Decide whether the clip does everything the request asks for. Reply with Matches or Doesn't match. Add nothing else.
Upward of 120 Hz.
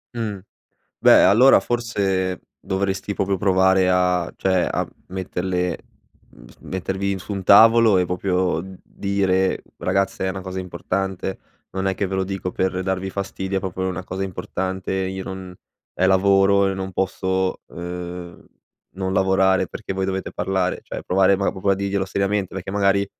Doesn't match